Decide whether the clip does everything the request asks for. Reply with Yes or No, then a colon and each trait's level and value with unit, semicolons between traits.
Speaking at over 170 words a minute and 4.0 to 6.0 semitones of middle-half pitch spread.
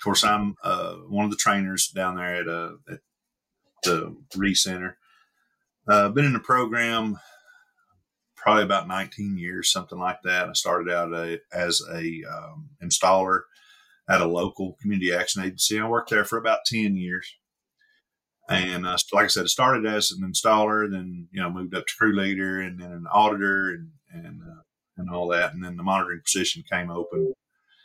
Yes: average, 180 wpm; average, 4.4 semitones